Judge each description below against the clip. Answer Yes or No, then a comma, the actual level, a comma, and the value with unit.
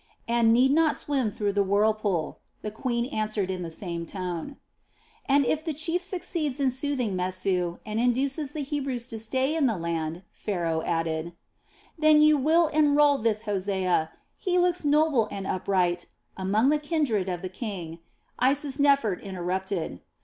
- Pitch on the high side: Yes, high, 220 Hz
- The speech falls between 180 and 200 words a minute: No, average, 155 wpm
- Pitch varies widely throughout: Yes, wide, 7.6 semitones